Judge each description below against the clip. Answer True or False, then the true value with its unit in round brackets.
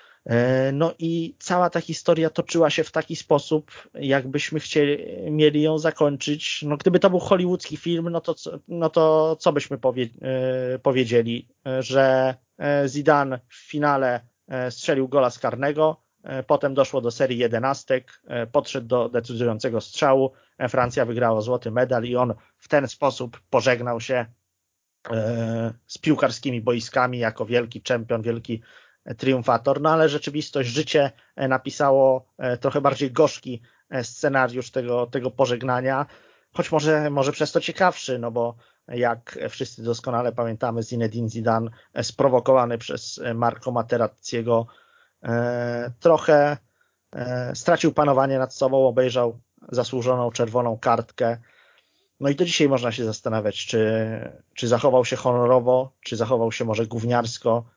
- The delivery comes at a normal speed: True (125 wpm)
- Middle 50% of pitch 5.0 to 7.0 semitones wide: False (3.6 semitones)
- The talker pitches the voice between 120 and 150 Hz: True (130 Hz)